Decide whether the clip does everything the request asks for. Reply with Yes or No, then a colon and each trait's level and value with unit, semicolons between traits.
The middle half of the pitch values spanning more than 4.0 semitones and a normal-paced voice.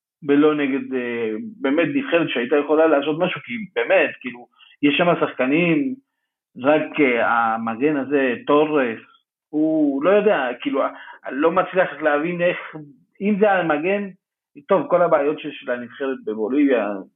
Yes: wide, 5.6 semitones; average, 120 wpm